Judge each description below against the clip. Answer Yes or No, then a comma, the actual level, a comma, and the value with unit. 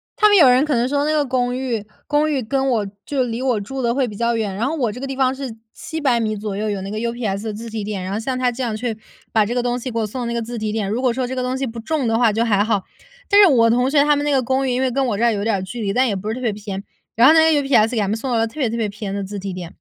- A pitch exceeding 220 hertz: Yes, high, 235 Hz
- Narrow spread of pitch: No, average, 3.6 semitones